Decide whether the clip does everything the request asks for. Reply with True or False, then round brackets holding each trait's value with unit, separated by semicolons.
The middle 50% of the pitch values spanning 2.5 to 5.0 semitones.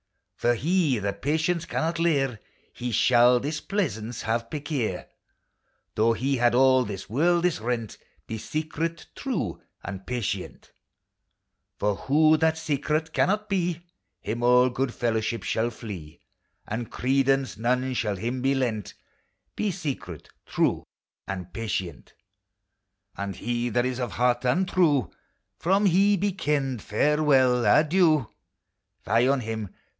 False (5.4 semitones)